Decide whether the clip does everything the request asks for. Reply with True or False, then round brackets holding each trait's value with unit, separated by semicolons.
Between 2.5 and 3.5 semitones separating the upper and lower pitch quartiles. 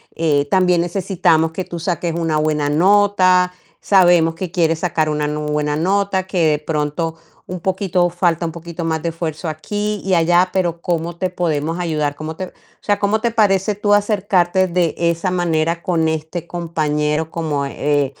True (2.8 semitones)